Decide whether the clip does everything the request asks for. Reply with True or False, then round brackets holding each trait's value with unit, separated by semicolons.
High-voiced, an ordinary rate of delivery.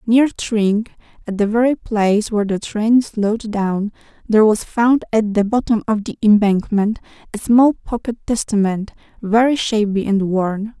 True (215 Hz; 155 wpm)